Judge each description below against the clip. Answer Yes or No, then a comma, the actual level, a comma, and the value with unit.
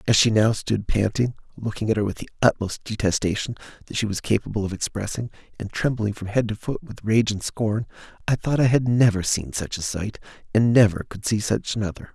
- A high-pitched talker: No, low, 110 Hz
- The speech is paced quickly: Yes, fast, 210 wpm